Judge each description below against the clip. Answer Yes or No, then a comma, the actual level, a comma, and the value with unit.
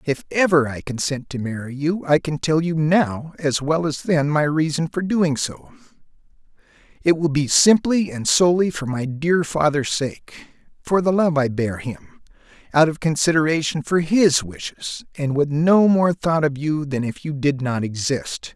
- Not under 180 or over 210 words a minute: Yes, average, 185 wpm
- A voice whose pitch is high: No, medium, 155 Hz